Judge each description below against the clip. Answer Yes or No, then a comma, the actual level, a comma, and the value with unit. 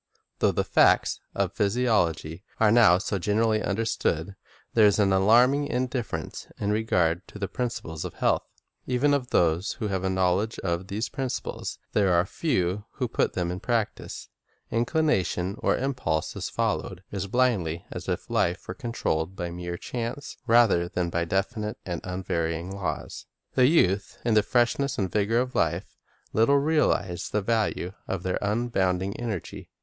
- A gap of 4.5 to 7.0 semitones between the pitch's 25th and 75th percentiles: Yes, average, 4.8 semitones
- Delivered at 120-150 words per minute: No, average, 160 wpm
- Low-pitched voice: Yes, low, 100 Hz